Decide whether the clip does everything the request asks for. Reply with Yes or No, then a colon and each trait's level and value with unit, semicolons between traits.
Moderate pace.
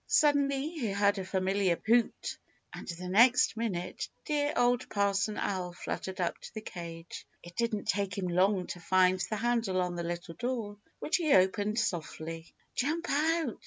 Yes: average, 165 wpm